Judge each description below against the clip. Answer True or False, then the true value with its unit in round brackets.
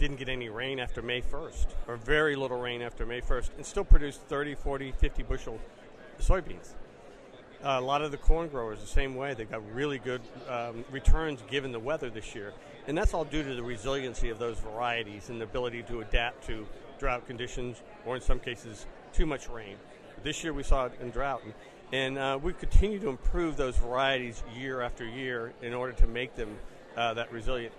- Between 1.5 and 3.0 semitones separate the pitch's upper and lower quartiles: True (2.7 semitones)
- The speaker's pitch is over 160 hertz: False (125 Hz)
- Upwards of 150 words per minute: True (205 wpm)